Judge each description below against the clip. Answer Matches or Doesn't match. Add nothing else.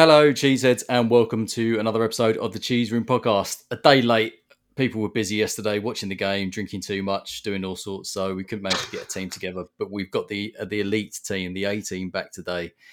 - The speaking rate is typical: Doesn't match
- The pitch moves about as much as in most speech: Matches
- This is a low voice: Matches